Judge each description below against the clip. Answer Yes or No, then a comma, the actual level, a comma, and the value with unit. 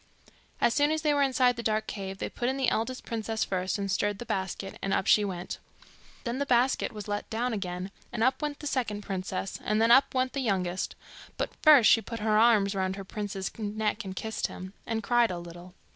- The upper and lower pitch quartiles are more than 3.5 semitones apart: Yes, average, 3.9 semitones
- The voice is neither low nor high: No, high, 215 Hz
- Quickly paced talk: Yes, fast, 225 wpm